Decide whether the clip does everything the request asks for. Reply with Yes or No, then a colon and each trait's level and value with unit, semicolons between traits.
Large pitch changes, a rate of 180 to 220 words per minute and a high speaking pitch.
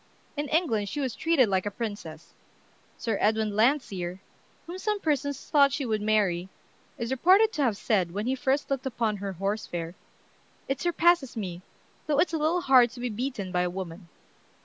Yes: wide, 6.3 semitones; average, 185 wpm; high, 235 Hz